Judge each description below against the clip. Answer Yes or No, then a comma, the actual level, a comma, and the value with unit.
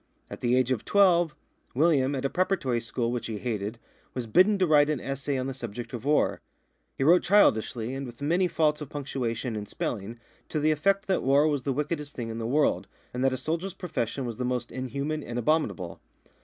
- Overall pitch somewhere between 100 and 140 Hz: Yes, low, 135 Hz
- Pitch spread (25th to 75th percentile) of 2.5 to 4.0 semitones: No, average, 4.4 semitones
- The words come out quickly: Yes, fast, 210 wpm